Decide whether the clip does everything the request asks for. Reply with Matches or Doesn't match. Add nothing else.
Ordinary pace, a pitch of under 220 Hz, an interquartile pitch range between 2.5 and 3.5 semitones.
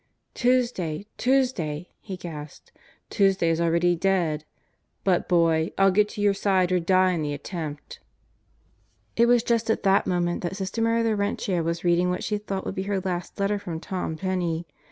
Matches